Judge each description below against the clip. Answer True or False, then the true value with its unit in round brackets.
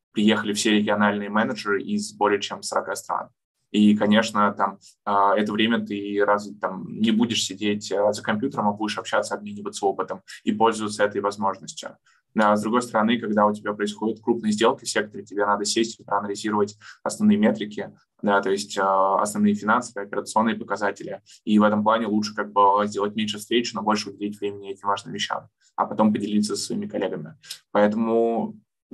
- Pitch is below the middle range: True (105 Hz)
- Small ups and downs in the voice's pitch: True (1.2 semitones)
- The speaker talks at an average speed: False (165 wpm)